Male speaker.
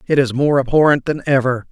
Yes: male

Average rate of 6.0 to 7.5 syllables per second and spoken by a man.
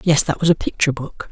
Yes: 6.6 syllables/s; male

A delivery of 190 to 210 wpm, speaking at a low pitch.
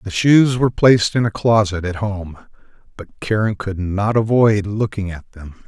No: average, 180 wpm; low, 105 Hz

